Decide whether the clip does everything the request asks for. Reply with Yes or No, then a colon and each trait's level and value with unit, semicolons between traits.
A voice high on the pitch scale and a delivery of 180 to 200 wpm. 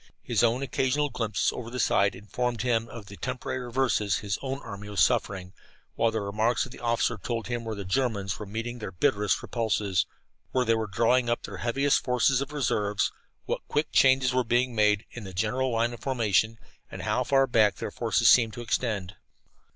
No: low, 115 Hz; average, 195 wpm